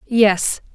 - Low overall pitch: No, high, 210 Hz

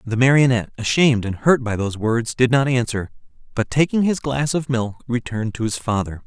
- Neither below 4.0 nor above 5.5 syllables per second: No, 5.7 syllables/s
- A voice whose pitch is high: No, low, 120 Hz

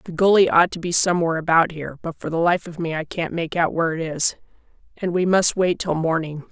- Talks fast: Yes, fast, 250 wpm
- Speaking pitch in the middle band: Yes, medium, 170 Hz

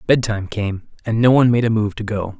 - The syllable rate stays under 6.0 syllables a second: No, 6.2 syllables/s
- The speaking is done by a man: Yes, male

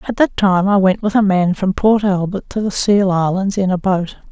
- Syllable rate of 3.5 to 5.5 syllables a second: Yes, 5.0 syllables/s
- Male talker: No, female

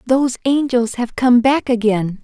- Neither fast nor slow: Yes, average, 160 wpm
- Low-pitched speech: No, high, 245 Hz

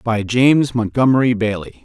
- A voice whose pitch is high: No, low, 120 Hz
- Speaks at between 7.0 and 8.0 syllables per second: No, 5.0 syllables/s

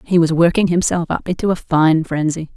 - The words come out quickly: Yes, fast, 210 wpm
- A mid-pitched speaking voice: Yes, medium, 165 Hz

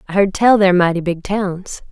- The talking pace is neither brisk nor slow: No, fast, 220 wpm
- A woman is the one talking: Yes, female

